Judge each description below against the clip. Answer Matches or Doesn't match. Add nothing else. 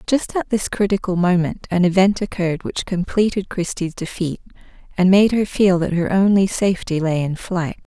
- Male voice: Doesn't match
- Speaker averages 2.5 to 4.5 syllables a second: Doesn't match